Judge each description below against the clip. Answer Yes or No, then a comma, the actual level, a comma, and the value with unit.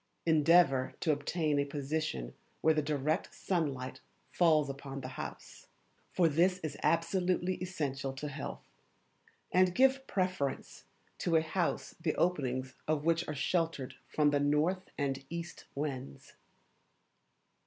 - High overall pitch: No, medium, 155 Hz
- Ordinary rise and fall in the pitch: Yes, average, 3.6 semitones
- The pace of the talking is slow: Yes, slow, 130 wpm